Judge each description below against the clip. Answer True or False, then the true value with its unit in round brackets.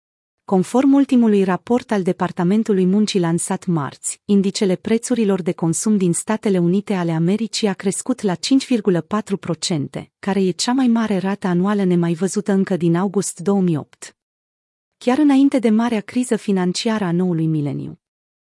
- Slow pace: False (140 wpm)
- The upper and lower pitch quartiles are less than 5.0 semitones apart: True (3.8 semitones)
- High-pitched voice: True (195 Hz)